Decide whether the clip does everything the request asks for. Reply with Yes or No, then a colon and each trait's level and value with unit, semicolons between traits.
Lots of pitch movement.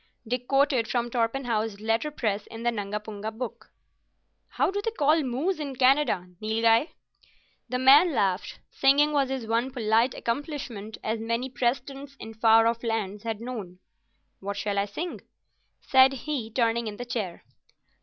No: average, 3.6 semitones